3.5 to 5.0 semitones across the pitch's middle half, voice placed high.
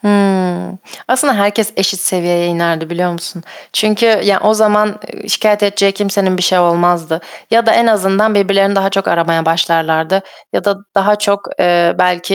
No: average, 2.9 semitones; high, 195 Hz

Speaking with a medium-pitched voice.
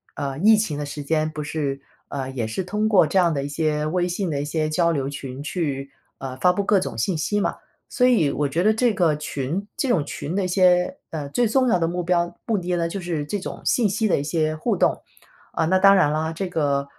Yes: medium, 165 Hz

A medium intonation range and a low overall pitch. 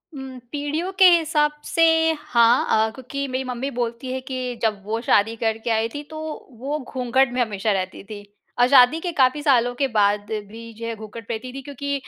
No: average, 3.9 semitones; very high, 250 Hz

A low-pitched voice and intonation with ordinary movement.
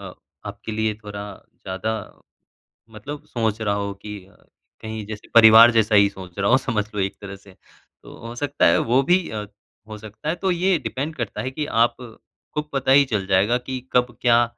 Yes: low, 110 Hz; average, 4.1 semitones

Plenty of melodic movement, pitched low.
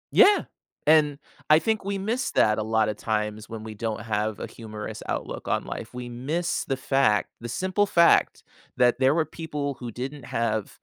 Yes: wide, 6.4 semitones; low, 125 Hz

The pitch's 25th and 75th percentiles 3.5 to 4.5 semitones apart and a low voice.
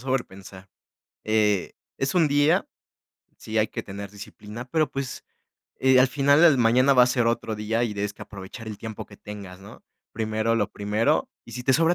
Yes: average, 4.1 semitones; low, 115 Hz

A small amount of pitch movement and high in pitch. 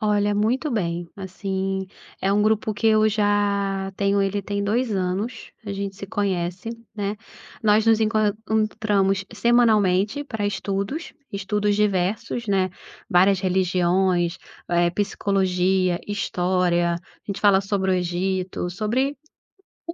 Yes: narrow, 2.2 semitones; high, 200 Hz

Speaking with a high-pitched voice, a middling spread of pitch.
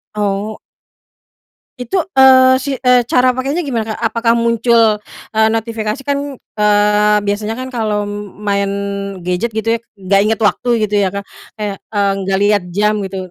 Yes: high, 215 Hz; average, 3.0 semitones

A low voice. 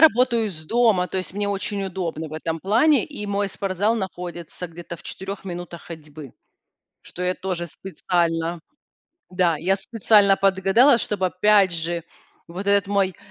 No: high, 190 Hz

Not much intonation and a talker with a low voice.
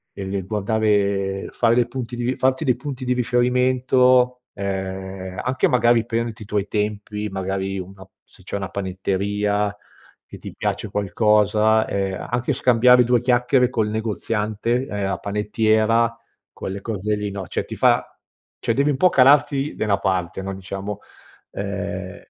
No: average, 3.9 semitones; low, 105 Hz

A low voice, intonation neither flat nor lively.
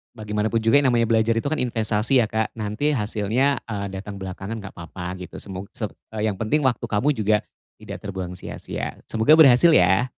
Yes: low, 110 Hz; average, 3.3 semitones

